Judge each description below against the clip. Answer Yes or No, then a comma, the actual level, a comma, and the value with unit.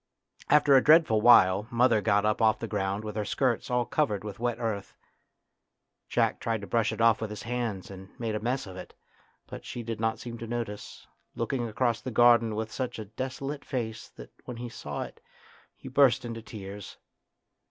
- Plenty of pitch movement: No, narrow, 2.4 semitones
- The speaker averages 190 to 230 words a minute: Yes, average, 195 wpm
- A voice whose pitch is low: Yes, low, 115 Hz